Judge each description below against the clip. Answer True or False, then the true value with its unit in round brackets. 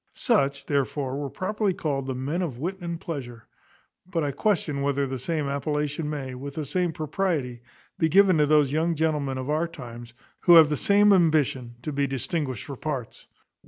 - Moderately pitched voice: True (150 Hz)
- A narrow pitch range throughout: False (3.6 semitones)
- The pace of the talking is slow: False (185 wpm)